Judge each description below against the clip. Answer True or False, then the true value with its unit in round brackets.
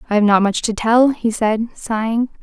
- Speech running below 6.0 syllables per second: True (4.9 syllables/s)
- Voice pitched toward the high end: True (225 Hz)